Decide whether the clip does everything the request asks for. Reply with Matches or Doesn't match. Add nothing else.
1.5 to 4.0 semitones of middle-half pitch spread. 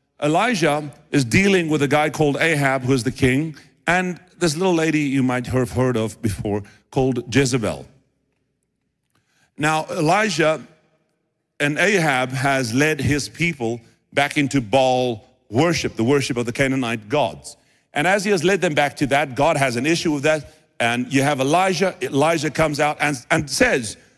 Matches